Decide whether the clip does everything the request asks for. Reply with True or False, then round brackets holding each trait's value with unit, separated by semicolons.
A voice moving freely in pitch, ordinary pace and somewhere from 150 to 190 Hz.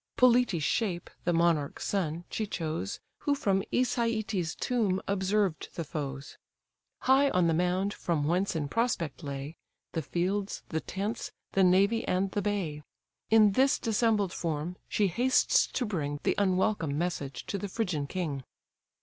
False (4.7 semitones; 150 wpm; 185 Hz)